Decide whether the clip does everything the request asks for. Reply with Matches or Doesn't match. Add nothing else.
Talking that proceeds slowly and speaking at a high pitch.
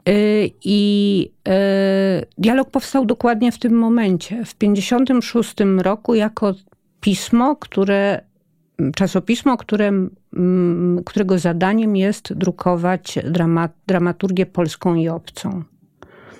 Matches